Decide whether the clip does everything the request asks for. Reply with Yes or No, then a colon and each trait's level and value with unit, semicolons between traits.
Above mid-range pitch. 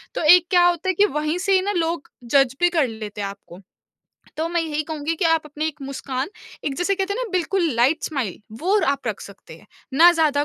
Yes: very high, 315 Hz